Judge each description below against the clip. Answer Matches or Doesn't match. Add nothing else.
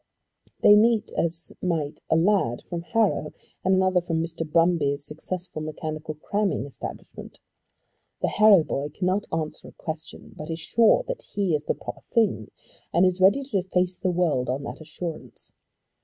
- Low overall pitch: Doesn't match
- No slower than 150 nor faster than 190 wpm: Matches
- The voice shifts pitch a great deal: Doesn't match